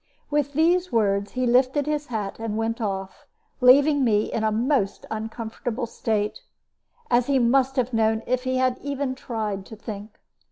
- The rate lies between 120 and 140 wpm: No, average, 165 wpm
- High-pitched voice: Yes, high, 240 Hz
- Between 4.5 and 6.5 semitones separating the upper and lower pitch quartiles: No, average, 3.4 semitones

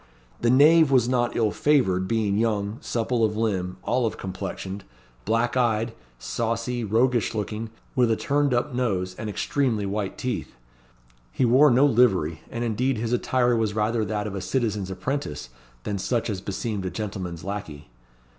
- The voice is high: No, low, 110 Hz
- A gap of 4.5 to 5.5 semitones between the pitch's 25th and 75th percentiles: No, average, 3.5 semitones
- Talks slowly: No, average, 160 wpm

